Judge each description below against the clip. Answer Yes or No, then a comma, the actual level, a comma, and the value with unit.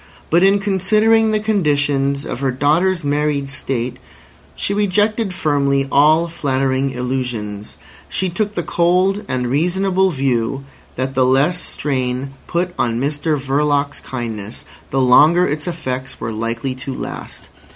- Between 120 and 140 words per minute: Yes, slow, 135 wpm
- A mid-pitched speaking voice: Yes, medium, 145 Hz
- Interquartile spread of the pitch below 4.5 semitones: No, wide, 5.4 semitones